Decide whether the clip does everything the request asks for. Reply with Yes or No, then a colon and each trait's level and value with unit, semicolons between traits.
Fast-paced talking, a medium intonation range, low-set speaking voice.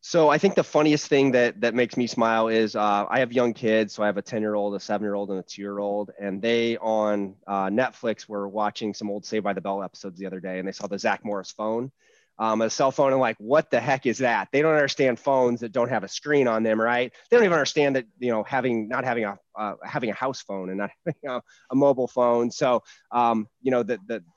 Yes: fast, 270 wpm; average, 3.8 semitones; low, 115 Hz